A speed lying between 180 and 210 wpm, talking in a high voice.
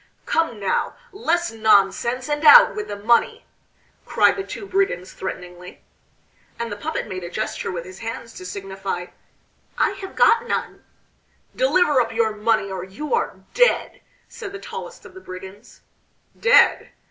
No: average, 155 wpm; high, 230 Hz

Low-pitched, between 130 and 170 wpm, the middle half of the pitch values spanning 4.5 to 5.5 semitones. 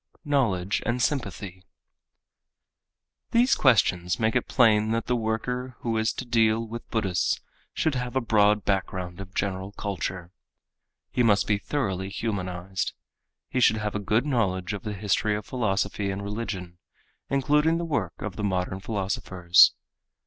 No: low, 105 Hz; average, 150 wpm; average, 3.7 semitones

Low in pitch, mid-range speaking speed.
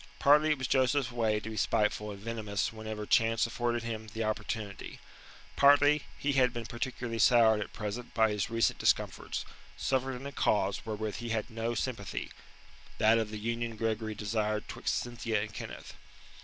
Yes: low, 115 Hz; average, 170 wpm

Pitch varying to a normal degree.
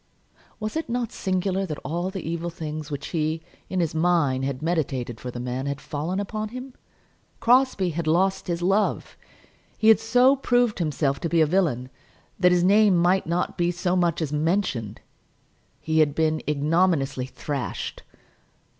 Yes: average, 4.3 semitones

